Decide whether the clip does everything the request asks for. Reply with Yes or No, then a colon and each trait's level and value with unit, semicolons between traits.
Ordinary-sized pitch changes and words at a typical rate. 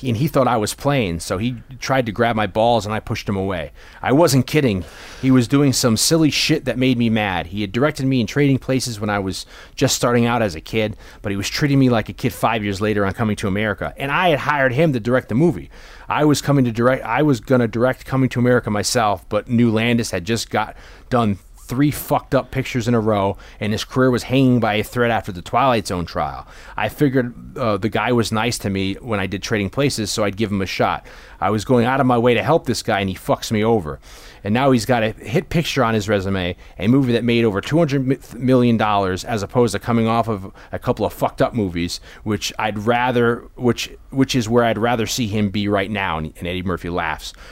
No: average, 3.9 semitones; fast, 245 wpm